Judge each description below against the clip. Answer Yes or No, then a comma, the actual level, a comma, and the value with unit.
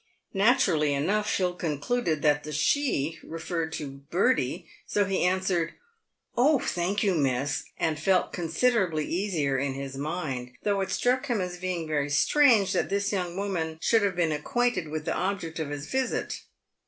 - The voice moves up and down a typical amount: Yes, average, 4.8 semitones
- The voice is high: No, medium, 175 Hz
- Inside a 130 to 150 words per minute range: No, average, 170 wpm